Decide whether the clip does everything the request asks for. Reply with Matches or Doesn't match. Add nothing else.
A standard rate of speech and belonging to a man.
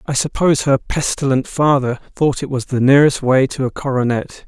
Matches